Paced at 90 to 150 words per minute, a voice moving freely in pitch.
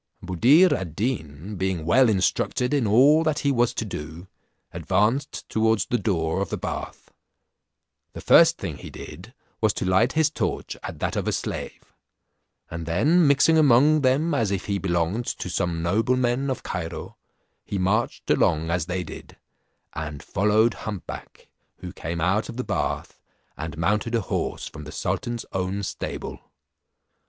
No: average, 160 wpm; wide, 6.1 semitones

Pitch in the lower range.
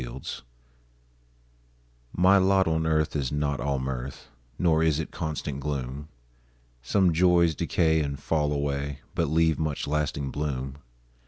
Yes: very low, 75 Hz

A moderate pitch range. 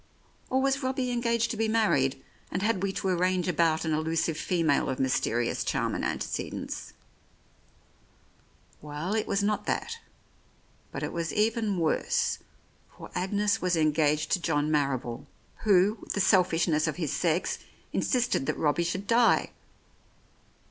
No: wide, 5.8 semitones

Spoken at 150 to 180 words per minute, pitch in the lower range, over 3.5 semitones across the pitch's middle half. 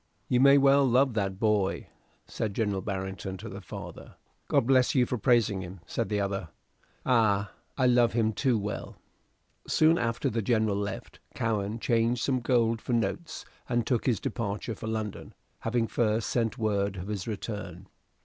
No: average, 170 wpm; low, 110 Hz; average, 3.2 semitones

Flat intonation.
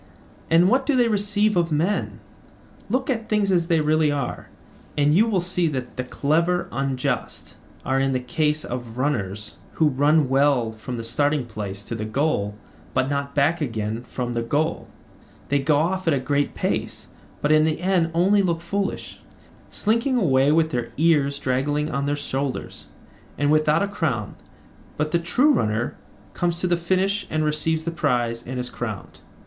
No: average, 4.8 semitones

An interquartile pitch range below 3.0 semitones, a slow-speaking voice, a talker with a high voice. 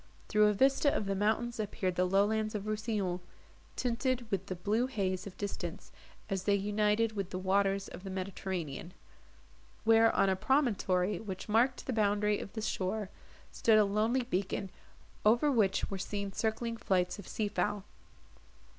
No: narrow, 2.5 semitones; average, 165 wpm; high, 205 Hz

